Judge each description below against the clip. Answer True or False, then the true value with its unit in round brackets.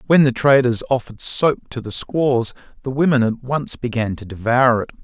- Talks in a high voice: False (125 Hz)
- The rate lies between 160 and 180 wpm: False (190 wpm)